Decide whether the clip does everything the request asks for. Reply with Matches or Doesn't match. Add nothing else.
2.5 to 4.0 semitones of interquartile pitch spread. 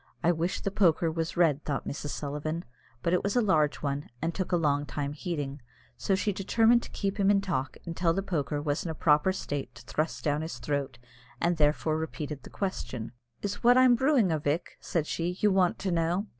Doesn't match